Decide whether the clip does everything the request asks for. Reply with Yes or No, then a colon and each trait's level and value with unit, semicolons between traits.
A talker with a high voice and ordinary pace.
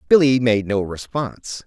No: low, 120 Hz; average, 145 wpm